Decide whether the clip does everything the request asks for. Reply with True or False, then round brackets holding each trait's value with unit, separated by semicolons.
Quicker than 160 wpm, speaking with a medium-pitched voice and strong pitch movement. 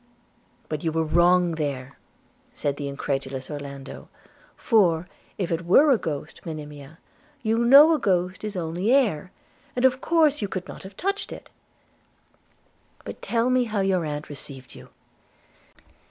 False (155 wpm; 175 Hz; 7.3 semitones)